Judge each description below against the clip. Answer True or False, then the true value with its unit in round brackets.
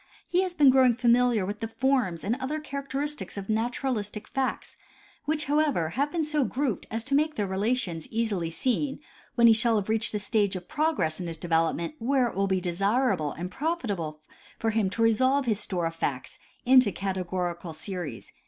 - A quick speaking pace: False (195 wpm)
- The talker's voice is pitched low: False (225 Hz)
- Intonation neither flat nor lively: False (6.2 semitones)